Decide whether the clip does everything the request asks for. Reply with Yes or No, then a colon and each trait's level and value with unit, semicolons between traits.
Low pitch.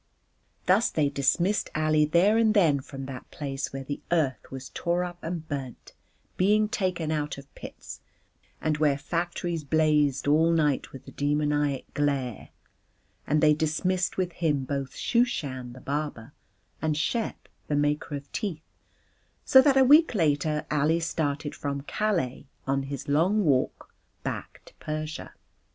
No: medium, 150 Hz